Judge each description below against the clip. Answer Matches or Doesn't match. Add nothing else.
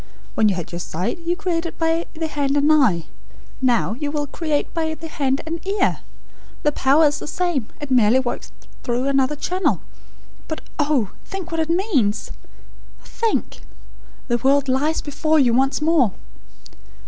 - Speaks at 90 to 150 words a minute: Doesn't match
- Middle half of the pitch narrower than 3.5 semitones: Doesn't match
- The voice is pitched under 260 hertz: Doesn't match